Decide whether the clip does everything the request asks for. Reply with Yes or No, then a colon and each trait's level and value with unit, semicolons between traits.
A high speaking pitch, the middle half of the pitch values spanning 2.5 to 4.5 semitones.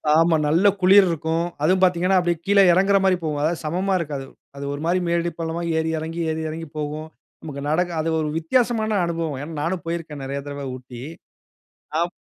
No: medium, 165 Hz; average, 2.9 semitones